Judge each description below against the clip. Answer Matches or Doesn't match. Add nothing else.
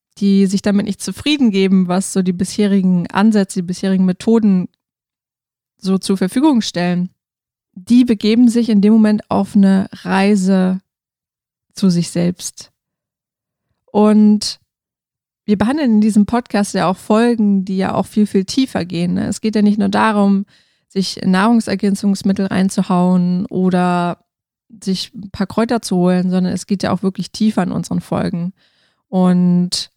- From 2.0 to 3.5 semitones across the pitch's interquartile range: Matches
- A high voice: Matches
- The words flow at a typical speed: Matches